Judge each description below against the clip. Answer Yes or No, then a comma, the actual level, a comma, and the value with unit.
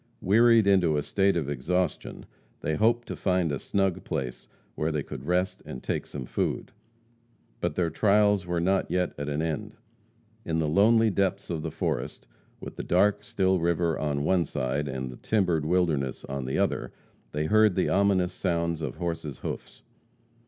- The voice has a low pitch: Yes, very low, 85 Hz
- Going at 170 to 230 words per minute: Yes, average, 175 wpm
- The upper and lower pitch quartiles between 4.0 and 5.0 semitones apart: Yes, average, 4.4 semitones